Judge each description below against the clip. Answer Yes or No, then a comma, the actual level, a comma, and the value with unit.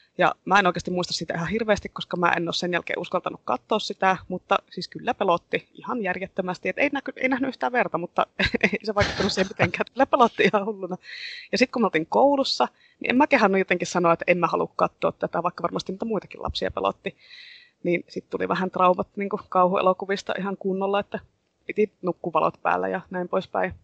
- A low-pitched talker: No, high, 195 Hz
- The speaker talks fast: Yes, fast, 205 wpm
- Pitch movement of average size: Yes, average, 4.0 semitones